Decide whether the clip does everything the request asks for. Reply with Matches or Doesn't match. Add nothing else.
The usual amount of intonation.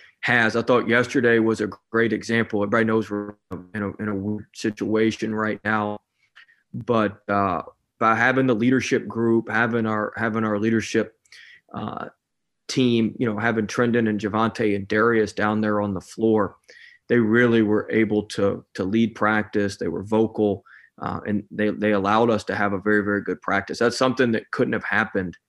Doesn't match